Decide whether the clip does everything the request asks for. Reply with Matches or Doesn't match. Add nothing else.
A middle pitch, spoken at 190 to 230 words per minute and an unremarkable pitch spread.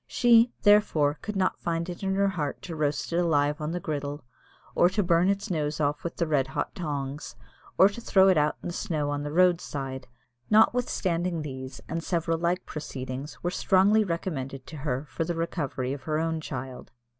Matches